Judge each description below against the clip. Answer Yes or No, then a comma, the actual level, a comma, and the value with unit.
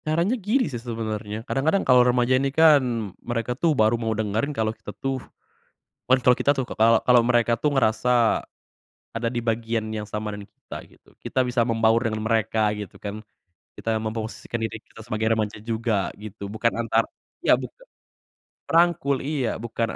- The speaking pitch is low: Yes, low, 115 Hz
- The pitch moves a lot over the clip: No, average, 2.7 semitones